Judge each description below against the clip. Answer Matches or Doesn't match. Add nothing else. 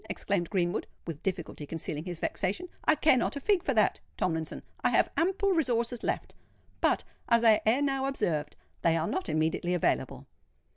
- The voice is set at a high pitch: Matches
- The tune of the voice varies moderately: Doesn't match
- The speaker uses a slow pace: Doesn't match